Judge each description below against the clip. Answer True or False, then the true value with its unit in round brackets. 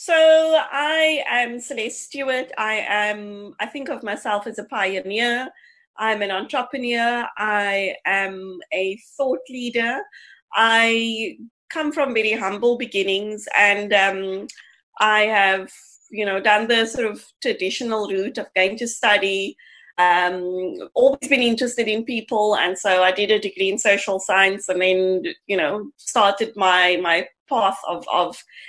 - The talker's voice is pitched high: True (215 Hz)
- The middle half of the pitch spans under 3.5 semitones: False (4.1 semitones)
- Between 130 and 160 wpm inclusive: True (145 wpm)